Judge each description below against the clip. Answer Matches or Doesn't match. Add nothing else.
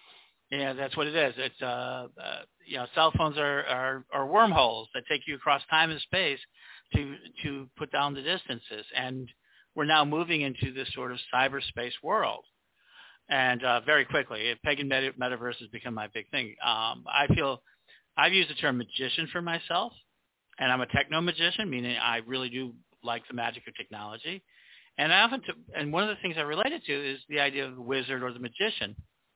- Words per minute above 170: Matches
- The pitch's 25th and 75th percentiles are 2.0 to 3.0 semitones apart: Doesn't match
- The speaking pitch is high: Doesn't match